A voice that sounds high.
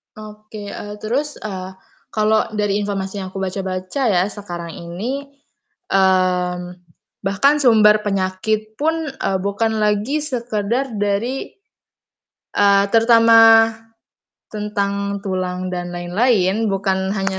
Yes: high, 205 Hz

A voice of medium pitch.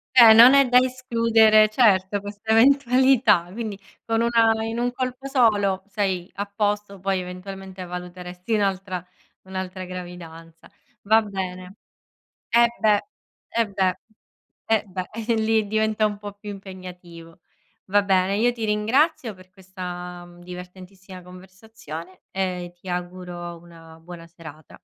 No: high, 195 Hz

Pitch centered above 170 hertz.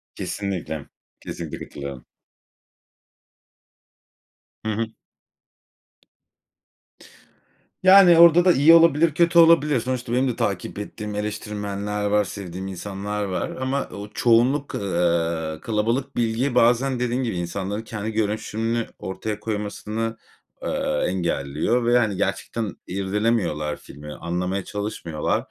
No: low, 105 Hz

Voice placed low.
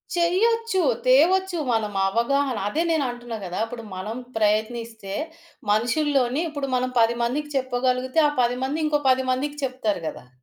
No: very high, 255 Hz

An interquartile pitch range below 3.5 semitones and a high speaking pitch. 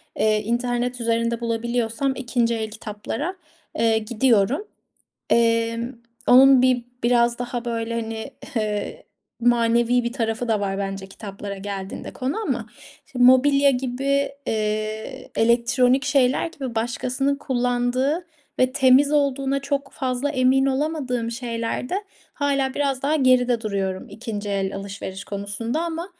Yes: average, 3.0 semitones; high, 245 Hz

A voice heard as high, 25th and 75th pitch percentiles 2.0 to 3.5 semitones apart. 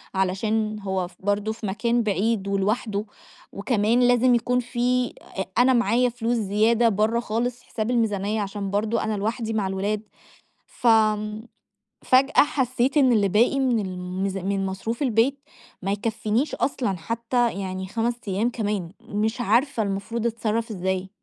Yes: high, 220 Hz; average, 3.1 semitones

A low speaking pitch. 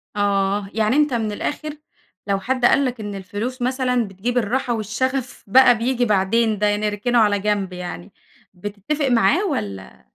No: high, 220 Hz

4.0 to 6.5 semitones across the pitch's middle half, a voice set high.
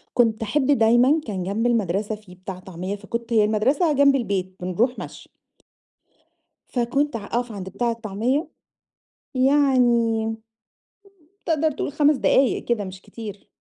Yes: average, 4.5 semitones; high, 230 Hz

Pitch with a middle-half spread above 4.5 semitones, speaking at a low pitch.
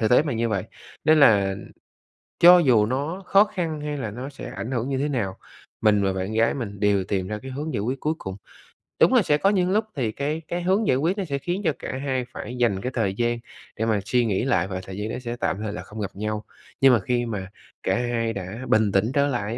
Yes: wide, 5.6 semitones; low, 120 Hz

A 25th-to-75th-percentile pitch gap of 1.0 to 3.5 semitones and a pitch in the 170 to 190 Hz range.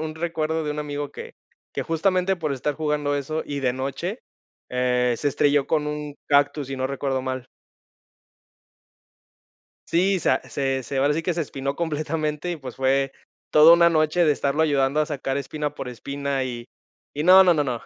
No: average, 2.7 semitones; medium, 145 Hz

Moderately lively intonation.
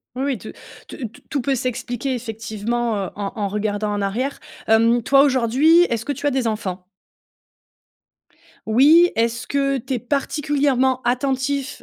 Yes: average, 3.8 semitones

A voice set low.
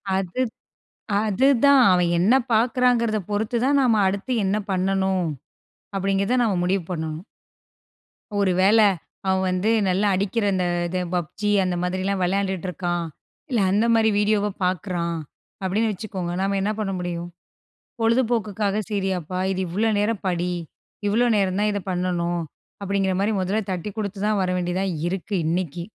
No: high, 195 Hz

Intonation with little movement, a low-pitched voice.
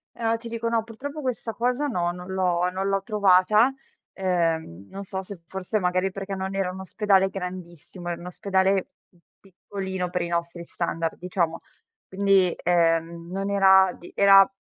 No: narrow, 2.1 semitones; high, 190 Hz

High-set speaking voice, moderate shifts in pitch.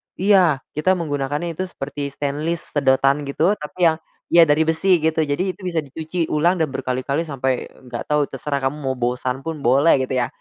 No: medium, 145 Hz; average, 3.4 semitones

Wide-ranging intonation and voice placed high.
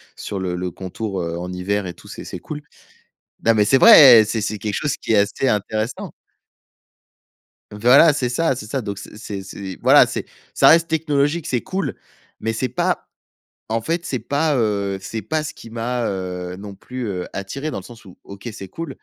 No: wide, 5.7 semitones; low, 110 Hz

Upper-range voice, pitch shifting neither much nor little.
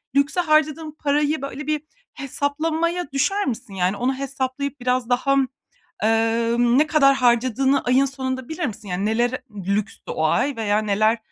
Yes: very high, 260 Hz; average, 4.0 semitones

